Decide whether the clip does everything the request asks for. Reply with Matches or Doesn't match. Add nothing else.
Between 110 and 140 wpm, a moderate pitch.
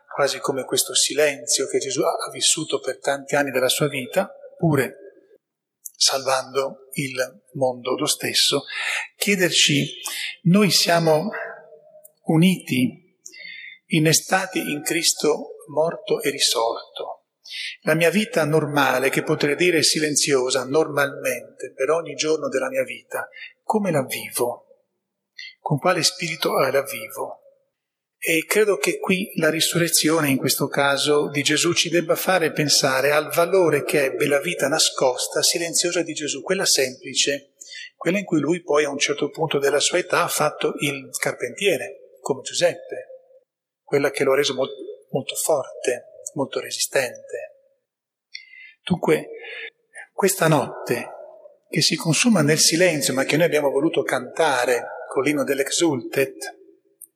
Matches